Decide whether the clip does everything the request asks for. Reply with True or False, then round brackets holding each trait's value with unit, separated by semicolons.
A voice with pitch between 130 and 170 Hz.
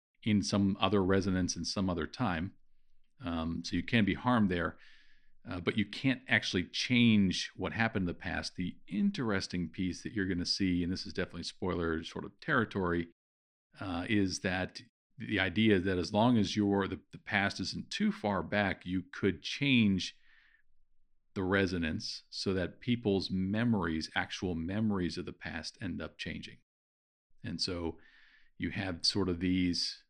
False (95 Hz)